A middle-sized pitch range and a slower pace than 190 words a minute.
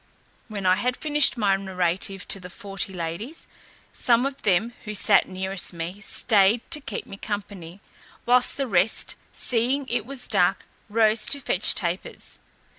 Yes: average, 4.3 semitones; average, 155 wpm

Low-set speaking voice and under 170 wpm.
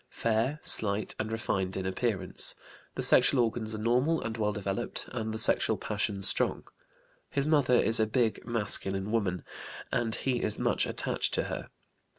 Yes: low, 110 Hz; average, 160 wpm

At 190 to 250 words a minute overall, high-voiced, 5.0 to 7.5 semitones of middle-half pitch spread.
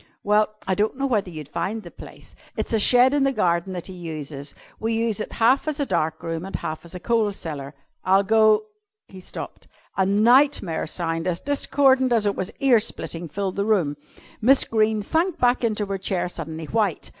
Yes: average, 200 wpm; high, 205 Hz; wide, 5.5 semitones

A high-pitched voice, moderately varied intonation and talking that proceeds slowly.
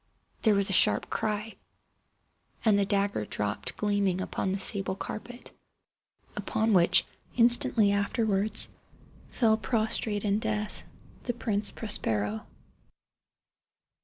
No: high, 205 Hz; narrow, 2.0 semitones; slow, 105 wpm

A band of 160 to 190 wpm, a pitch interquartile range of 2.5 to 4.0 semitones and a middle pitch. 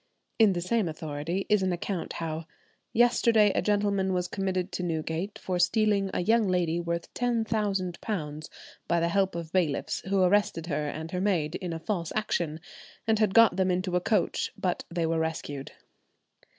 Yes: average, 170 wpm; average, 3.6 semitones; medium, 180 Hz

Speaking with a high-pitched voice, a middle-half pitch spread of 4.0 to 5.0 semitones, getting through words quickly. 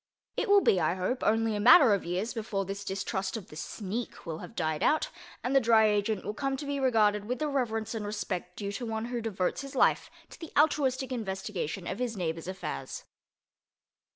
Yes: high, 215 Hz; average, 4.6 semitones; fast, 210 wpm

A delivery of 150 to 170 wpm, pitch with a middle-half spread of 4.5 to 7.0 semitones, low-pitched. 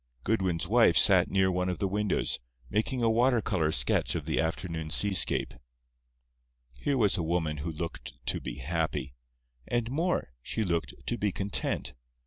Yes: average, 155 wpm; average, 5.2 semitones; very low, 95 Hz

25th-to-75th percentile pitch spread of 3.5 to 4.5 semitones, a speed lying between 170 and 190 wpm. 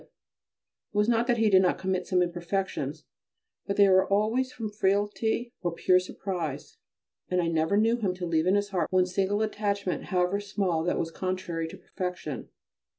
No: narrow, 2.5 semitones; average, 180 wpm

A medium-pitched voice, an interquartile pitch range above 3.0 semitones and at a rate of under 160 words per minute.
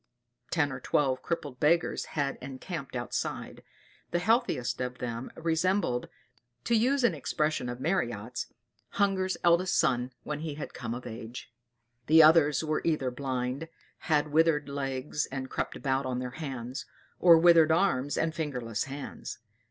Yes: medium, 145 Hz; average, 4.4 semitones; average, 145 wpm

